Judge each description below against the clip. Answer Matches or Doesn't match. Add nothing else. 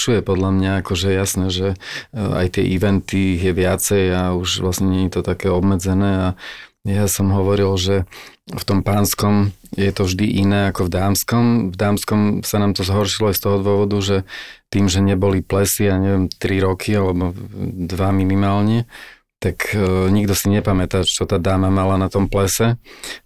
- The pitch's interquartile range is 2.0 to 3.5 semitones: Doesn't match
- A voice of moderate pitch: Doesn't match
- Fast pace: Matches